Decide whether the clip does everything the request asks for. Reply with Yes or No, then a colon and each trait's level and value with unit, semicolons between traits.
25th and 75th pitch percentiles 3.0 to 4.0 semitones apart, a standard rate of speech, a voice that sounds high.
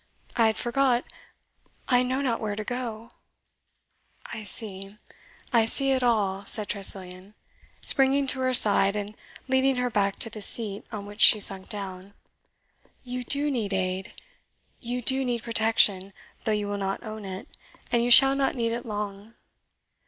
Yes: average, 3.7 semitones; average, 165 wpm; high, 220 Hz